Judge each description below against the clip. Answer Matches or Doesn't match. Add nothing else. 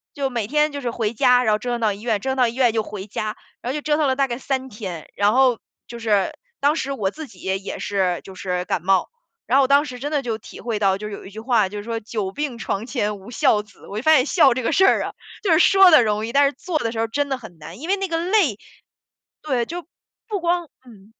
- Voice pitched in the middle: Doesn't match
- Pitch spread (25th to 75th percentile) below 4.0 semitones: Doesn't match